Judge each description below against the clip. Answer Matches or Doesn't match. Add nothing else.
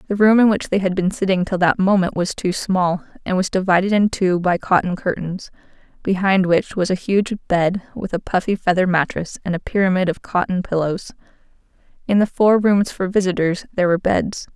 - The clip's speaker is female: Matches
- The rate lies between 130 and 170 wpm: Doesn't match